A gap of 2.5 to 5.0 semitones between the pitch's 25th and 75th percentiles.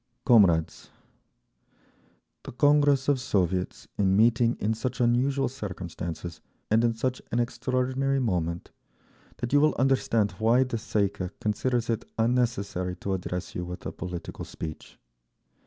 No: wide, 5.5 semitones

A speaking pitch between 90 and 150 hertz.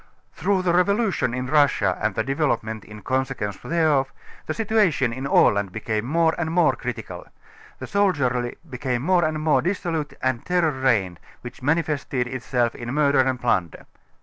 Yes: low, 135 Hz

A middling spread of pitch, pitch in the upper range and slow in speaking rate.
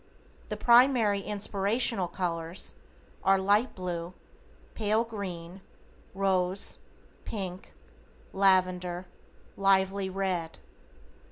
No: narrow, 2.1 semitones; high, 195 Hz; slow, 75 wpm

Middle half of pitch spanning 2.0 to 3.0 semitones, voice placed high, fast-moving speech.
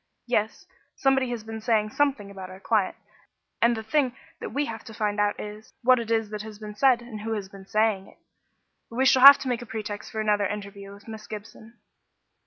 Yes: narrow, 2.4 semitones; high, 220 Hz; fast, 215 wpm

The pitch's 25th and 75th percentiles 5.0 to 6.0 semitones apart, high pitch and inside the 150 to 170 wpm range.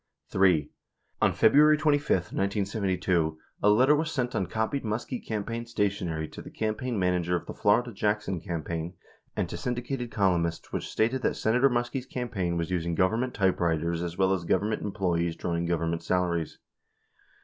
No: wide, 5.4 semitones; very low, 95 Hz; average, 160 wpm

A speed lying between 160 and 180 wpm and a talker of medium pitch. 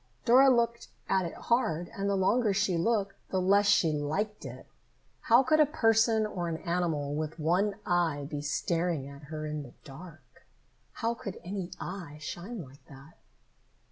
Yes: average, 170 wpm; medium, 180 Hz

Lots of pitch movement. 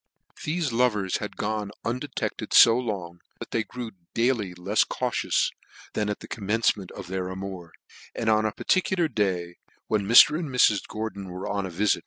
No: average, 3.6 semitones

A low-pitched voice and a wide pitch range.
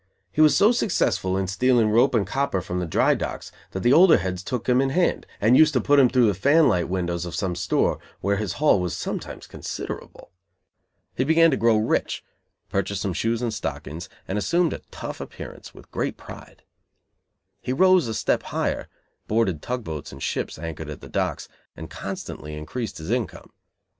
Yes: low, 110 Hz; wide, 6.6 semitones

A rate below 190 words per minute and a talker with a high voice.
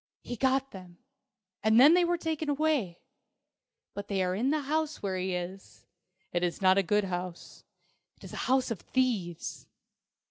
Yes: average, 175 wpm; high, 210 Hz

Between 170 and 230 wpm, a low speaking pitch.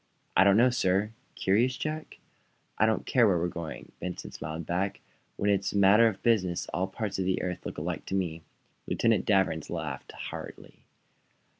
Yes: average, 175 wpm; very low, 95 Hz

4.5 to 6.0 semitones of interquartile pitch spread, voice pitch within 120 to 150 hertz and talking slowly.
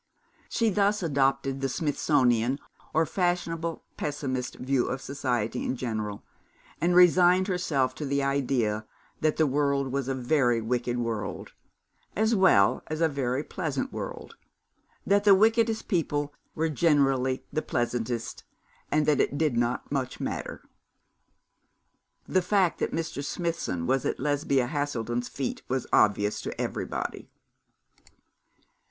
Yes: average, 4.8 semitones; medium, 140 Hz; slow, 130 wpm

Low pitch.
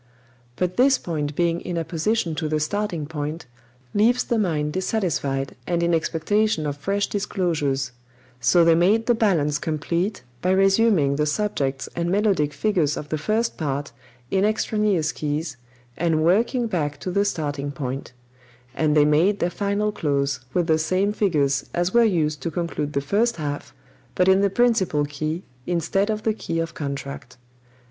No: medium, 170 Hz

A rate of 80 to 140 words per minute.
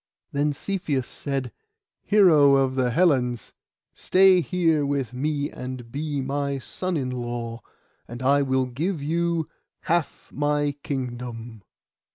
Yes: slow, 135 wpm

